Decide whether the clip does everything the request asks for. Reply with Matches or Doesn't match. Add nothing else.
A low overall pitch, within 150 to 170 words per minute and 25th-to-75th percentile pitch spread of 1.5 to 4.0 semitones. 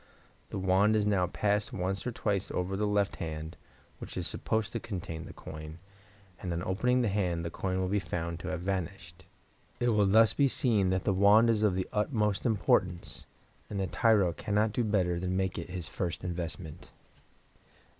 Doesn't match